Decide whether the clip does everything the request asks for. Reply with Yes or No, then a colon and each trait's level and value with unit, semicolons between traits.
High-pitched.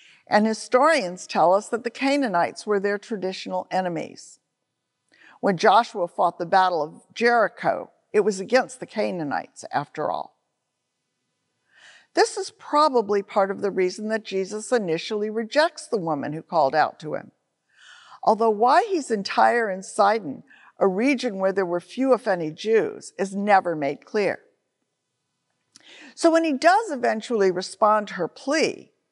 Yes: high, 215 Hz